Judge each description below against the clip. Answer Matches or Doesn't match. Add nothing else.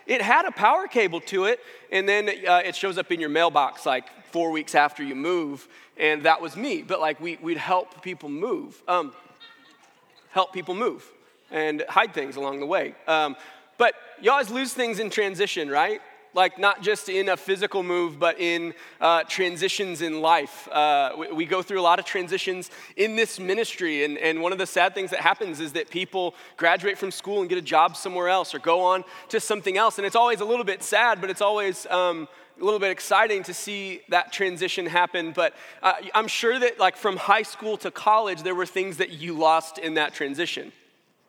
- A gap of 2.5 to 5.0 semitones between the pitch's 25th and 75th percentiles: Matches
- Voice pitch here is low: Doesn't match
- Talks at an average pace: Doesn't match